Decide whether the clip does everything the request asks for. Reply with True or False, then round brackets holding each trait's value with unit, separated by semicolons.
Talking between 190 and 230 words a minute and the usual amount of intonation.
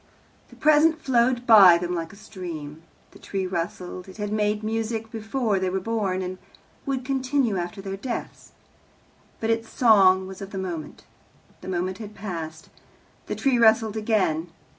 False (160 wpm; 3.6 semitones)